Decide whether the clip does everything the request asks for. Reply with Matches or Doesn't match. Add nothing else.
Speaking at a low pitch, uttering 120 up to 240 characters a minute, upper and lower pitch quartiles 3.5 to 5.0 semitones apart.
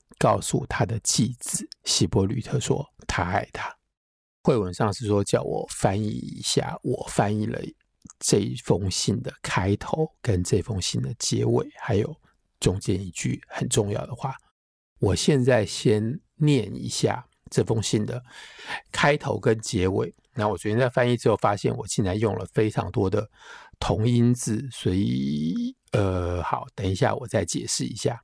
Matches